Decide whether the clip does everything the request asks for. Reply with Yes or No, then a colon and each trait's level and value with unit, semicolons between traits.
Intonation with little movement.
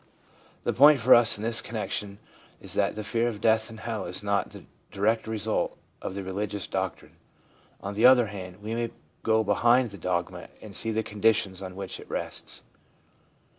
Yes: narrow, 2.3 semitones